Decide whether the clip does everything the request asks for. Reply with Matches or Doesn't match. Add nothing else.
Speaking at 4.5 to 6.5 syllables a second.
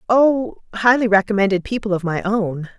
Matches